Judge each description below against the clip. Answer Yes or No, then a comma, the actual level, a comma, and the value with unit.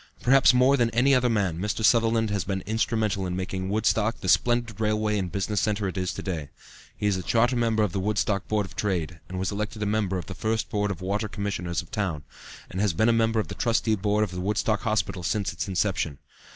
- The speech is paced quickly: Yes, fast, 240 wpm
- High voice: No, low, 105 Hz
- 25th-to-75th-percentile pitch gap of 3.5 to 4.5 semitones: No, average, 2.8 semitones